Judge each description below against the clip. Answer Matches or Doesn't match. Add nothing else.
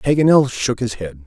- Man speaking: Matches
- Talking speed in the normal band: Matches